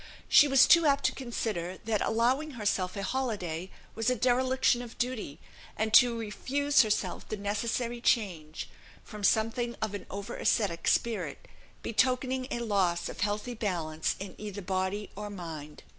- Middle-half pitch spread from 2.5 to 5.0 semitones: Yes, average, 4.1 semitones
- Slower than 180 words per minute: Yes, average, 155 wpm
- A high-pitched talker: Yes, high, 215 Hz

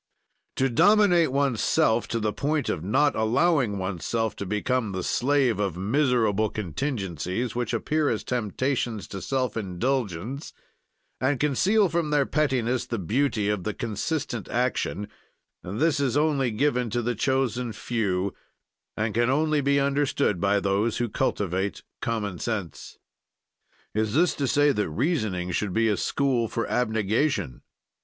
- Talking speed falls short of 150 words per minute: Yes, average, 140 wpm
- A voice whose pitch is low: Yes, low, 120 Hz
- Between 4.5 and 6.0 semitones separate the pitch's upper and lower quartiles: Yes, average, 5.2 semitones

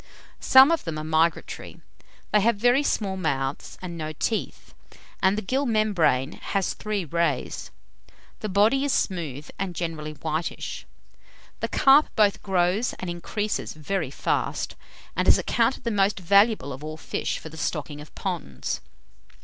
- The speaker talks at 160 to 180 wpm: No, average, 150 wpm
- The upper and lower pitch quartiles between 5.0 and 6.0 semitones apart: Yes, wide, 5.5 semitones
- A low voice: No, medium, 185 Hz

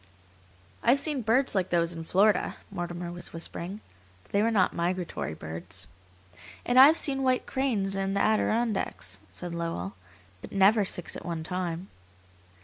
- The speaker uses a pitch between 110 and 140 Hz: No, medium, 185 Hz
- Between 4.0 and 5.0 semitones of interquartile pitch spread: Yes, average, 4.6 semitones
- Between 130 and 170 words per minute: Yes, average, 155 wpm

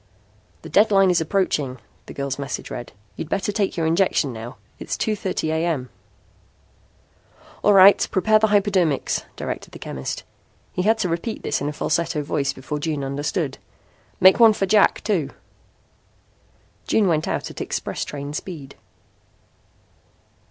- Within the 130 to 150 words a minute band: Yes, average, 145 wpm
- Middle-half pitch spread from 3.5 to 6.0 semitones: Yes, wide, 5.6 semitones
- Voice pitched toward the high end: No, medium, 165 Hz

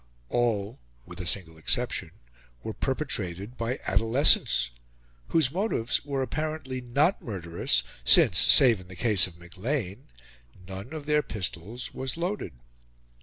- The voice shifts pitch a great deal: Yes, wide, 7.1 semitones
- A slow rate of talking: Yes, slow, 125 wpm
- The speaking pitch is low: Yes, low, 115 Hz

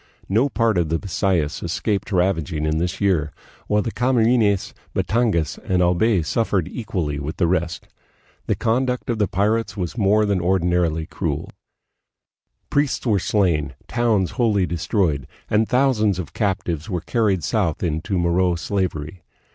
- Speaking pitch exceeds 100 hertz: No, very low, 95 Hz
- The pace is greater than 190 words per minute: No, average, 145 wpm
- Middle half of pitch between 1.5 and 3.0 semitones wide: No, average, 4.4 semitones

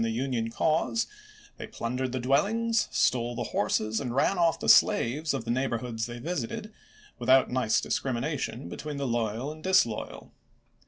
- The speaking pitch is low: Yes, low, 130 Hz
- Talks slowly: No, average, 160 wpm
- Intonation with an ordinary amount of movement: Yes, average, 4.6 semitones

